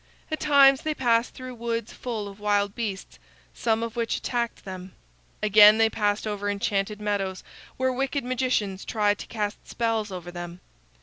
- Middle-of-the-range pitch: No, high, 215 Hz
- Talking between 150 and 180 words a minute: Yes, average, 165 wpm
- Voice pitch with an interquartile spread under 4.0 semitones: Yes, average, 2.8 semitones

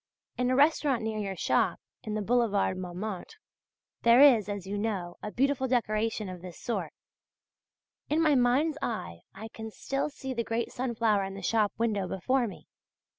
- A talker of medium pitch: No, high, 225 Hz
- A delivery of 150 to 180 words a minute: Yes, average, 175 wpm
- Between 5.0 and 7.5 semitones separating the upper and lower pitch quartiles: No, average, 4.1 semitones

